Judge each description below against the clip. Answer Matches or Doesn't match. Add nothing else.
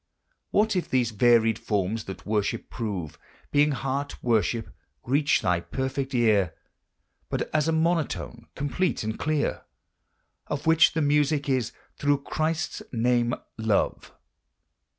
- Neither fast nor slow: Doesn't match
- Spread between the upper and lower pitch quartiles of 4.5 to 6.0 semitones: Matches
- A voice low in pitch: Matches